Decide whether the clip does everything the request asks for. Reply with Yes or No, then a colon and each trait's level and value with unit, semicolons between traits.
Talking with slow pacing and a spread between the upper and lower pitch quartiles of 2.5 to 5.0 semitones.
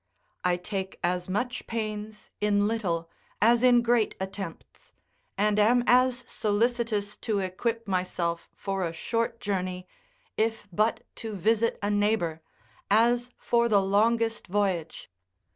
Yes: slow, 125 wpm; average, 3.3 semitones